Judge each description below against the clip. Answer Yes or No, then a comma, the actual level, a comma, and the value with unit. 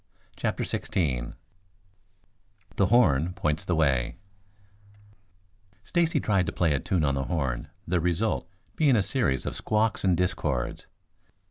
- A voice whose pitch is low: Yes, very low, 90 Hz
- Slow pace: Yes, slow, 130 wpm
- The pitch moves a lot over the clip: Yes, wide, 6.3 semitones